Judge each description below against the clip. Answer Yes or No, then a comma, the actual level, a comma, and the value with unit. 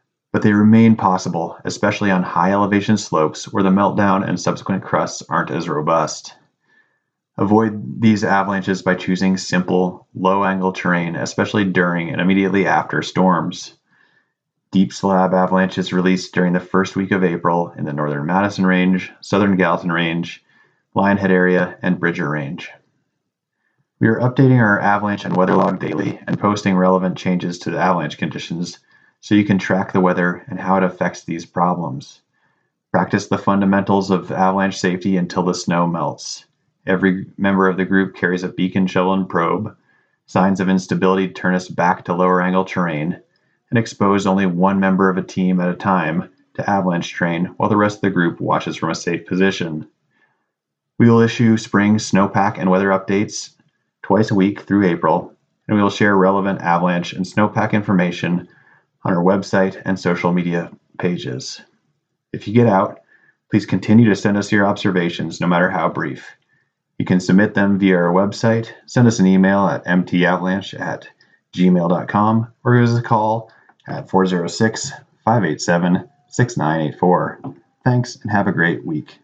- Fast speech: No, average, 160 wpm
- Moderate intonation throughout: No, narrow, 2.0 semitones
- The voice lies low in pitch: Yes, very low, 95 Hz